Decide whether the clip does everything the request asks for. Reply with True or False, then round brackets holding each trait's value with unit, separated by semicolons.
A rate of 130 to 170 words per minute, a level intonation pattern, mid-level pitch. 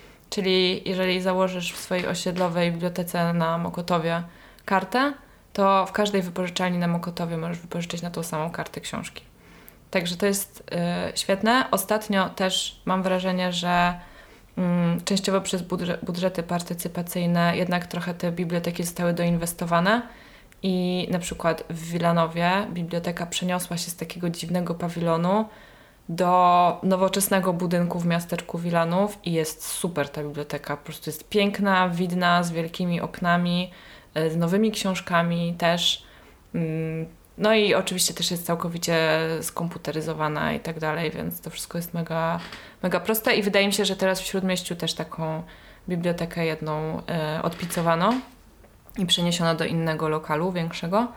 True (135 wpm; 1.8 semitones; 175 Hz)